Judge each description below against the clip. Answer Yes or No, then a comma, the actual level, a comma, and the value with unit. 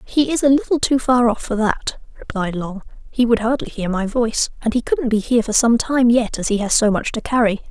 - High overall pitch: Yes, high, 230 Hz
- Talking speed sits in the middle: No, fast, 255 wpm